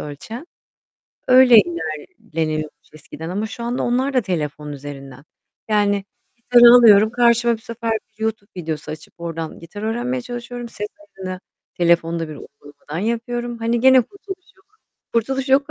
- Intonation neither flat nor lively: No, wide, 6.7 semitones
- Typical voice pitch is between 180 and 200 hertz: No, high, 220 Hz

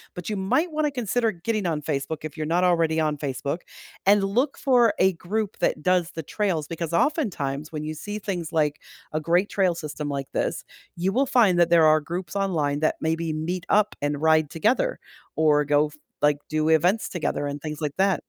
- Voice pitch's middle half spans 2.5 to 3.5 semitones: No, average, 4.5 semitones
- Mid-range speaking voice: Yes, medium, 170 Hz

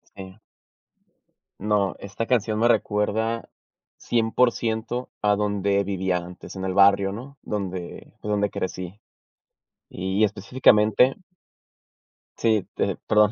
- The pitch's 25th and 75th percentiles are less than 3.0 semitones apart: Yes, narrow, 2.5 semitones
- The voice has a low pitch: Yes, low, 105 Hz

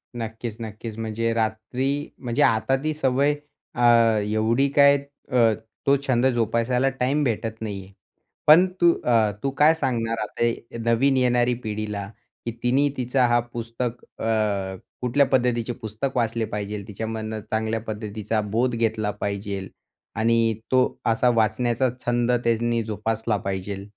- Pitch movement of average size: No, narrow, 2.3 semitones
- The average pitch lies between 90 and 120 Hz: Yes, low, 115 Hz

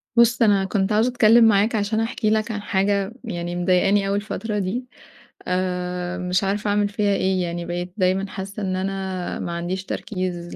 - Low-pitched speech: No, high, 195 Hz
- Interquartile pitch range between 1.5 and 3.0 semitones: Yes, narrow, 2.6 semitones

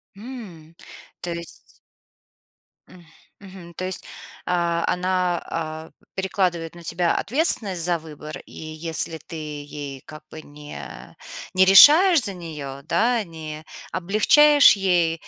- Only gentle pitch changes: No, average, 3.3 semitones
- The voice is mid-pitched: Yes, medium, 170 Hz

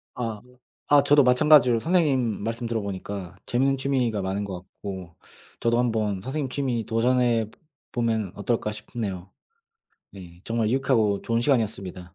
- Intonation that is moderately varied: Yes, average, 3.9 semitones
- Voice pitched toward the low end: Yes, low, 115 Hz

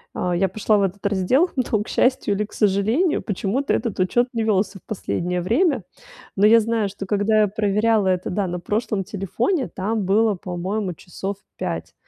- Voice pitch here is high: Yes, high, 205 Hz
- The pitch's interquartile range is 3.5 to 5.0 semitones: No, average, 2.9 semitones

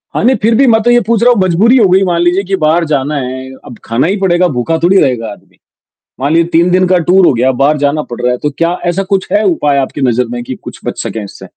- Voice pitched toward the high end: No, medium, 170 Hz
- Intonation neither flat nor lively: No, wide, 6.5 semitones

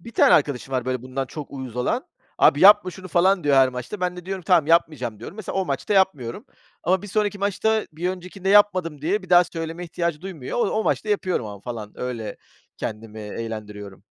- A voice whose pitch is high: No, medium, 165 Hz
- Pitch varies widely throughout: Yes, wide, 6.9 semitones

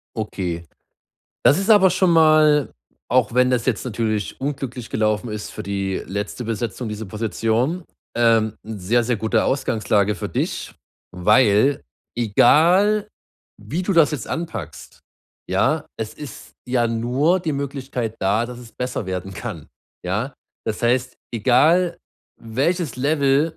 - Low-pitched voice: Yes, low, 120 Hz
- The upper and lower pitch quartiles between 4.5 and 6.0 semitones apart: Yes, average, 5.2 semitones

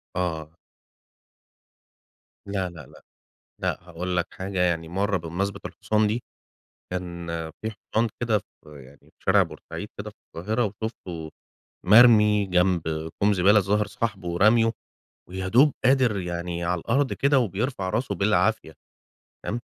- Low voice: Yes, very low, 95 Hz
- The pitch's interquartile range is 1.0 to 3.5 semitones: No, average, 3.9 semitones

